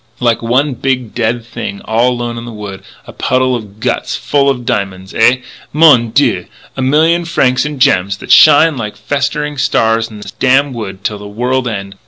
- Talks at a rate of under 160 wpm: No, average, 190 wpm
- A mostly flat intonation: No, average, 4.1 semitones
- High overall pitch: No, low, 120 Hz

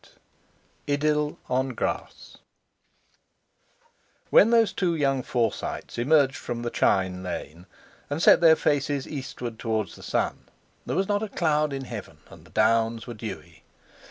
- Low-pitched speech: Yes, low, 130 Hz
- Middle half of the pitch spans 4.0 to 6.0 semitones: Yes, average, 5.0 semitones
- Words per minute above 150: No, average, 140 wpm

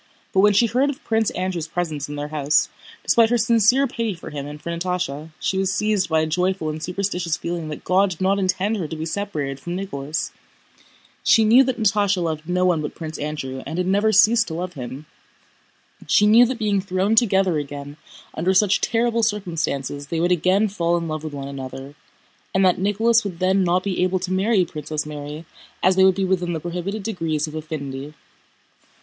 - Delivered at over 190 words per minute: Yes, fast, 205 wpm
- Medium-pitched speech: Yes, medium, 180 Hz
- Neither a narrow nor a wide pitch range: Yes, average, 4.5 semitones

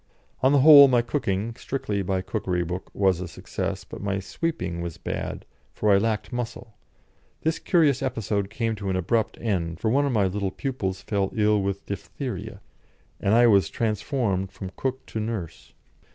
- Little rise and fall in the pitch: No, average, 4.1 semitones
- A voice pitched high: No, low, 105 Hz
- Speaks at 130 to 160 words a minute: No, average, 175 wpm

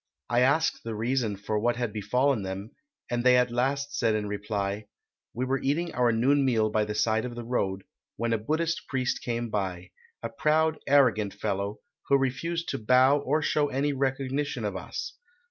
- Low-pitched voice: Yes, low, 120 Hz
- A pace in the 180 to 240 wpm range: Yes, average, 185 wpm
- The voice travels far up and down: No, average, 4.3 semitones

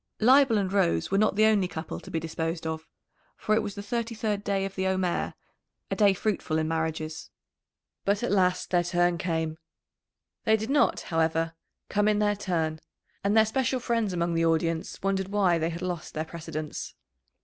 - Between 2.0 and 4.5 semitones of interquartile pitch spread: Yes, average, 4.2 semitones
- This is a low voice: No, medium, 185 Hz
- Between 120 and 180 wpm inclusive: No, average, 190 wpm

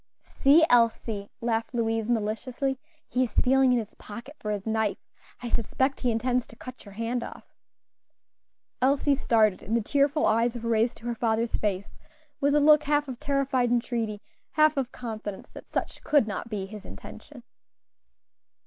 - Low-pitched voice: No, high, 235 Hz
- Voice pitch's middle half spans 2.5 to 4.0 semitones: Yes, average, 3.3 semitones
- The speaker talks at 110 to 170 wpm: Yes, average, 165 wpm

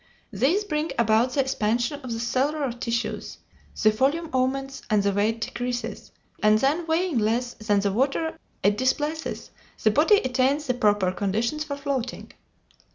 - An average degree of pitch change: Yes, average, 4.7 semitones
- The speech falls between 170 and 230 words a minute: No, average, 155 wpm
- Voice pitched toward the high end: Yes, very high, 250 Hz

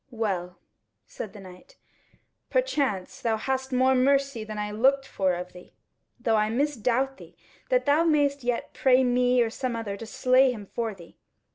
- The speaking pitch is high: Yes, high, 245 Hz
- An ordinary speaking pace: Yes, average, 170 wpm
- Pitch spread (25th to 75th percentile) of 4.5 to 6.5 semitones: No, average, 4.1 semitones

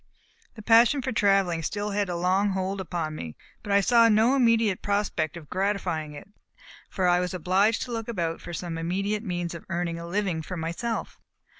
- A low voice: No, high, 190 Hz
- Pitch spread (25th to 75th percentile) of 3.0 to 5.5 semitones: Yes, average, 3.6 semitones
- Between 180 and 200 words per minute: Yes, average, 190 wpm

